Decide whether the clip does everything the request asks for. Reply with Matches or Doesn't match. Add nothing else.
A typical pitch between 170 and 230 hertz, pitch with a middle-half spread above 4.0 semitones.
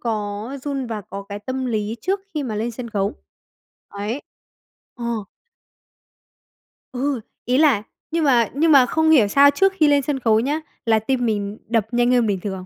Doesn't match